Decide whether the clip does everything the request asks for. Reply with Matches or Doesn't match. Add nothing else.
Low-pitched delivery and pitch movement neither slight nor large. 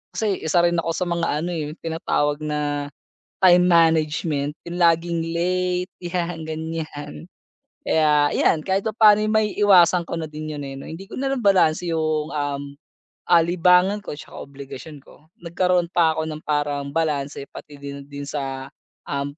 Doesn't match